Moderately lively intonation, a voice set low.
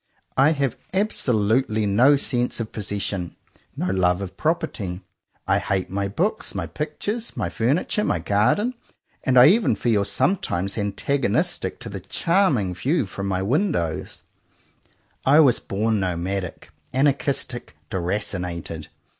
No: wide, 6.7 semitones; low, 110 Hz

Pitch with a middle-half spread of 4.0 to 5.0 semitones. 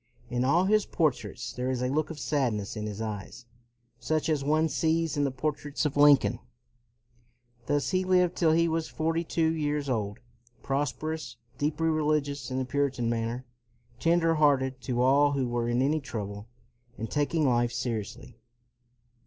Yes: average, 4.3 semitones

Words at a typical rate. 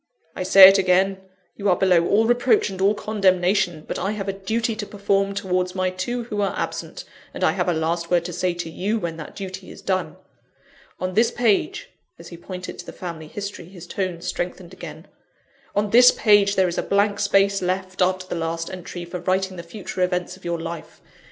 No: fast, 215 wpm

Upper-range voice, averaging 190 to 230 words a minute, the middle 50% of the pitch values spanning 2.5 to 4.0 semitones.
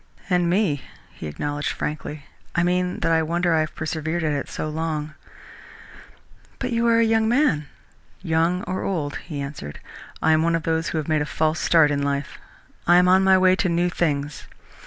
No: medium, 160 Hz; average, 200 wpm; average, 3.1 semitones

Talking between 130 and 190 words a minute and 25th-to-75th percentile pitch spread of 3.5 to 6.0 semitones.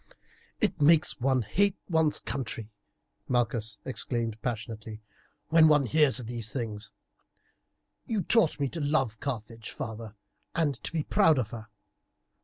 Yes: slow, 135 wpm; wide, 5.6 semitones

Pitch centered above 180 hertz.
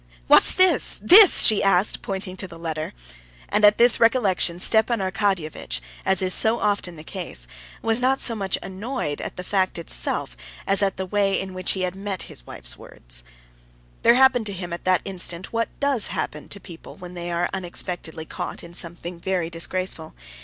Yes: high, 190 Hz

